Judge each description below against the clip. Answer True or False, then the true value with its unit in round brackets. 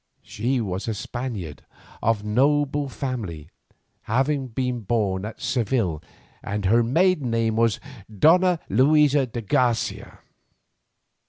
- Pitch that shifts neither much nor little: True (4.3 semitones)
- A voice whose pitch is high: False (120 Hz)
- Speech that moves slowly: True (110 wpm)